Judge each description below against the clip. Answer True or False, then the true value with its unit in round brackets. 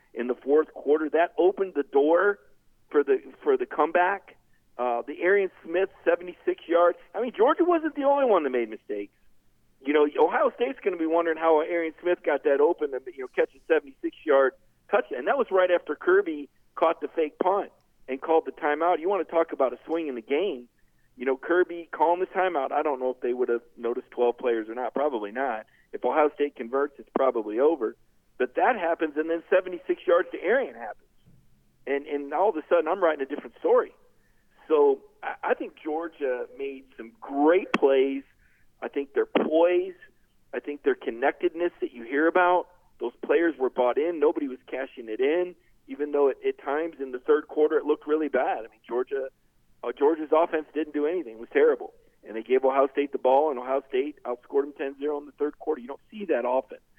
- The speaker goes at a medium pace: False (215 wpm)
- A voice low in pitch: False (170 Hz)